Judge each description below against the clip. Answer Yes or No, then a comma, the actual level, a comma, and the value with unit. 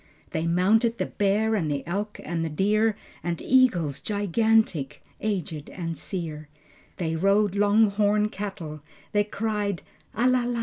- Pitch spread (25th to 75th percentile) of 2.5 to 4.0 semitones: No, average, 4.4 semitones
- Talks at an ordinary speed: Yes, average, 145 wpm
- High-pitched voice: Yes, high, 200 Hz